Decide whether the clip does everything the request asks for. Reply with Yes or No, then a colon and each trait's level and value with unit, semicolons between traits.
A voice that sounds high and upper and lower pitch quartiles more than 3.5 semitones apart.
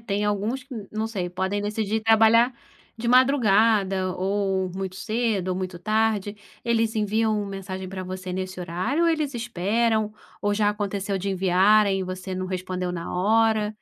No: high, 205 Hz; average, 3.0 semitones